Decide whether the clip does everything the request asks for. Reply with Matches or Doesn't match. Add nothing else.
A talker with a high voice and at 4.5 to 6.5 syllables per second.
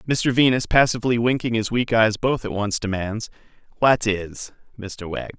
Doesn't match